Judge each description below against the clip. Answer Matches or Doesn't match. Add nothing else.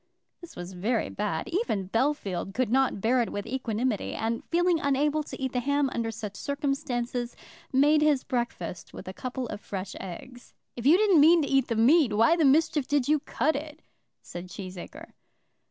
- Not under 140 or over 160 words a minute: Doesn't match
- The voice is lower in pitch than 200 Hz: Doesn't match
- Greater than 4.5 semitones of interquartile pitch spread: Matches